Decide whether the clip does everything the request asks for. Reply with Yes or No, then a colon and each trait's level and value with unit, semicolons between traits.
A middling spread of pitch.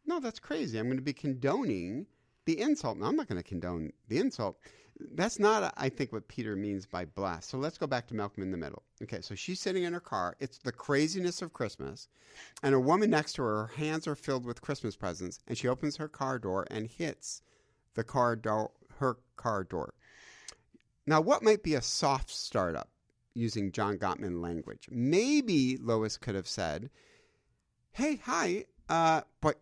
No: wide, 6.5 semitones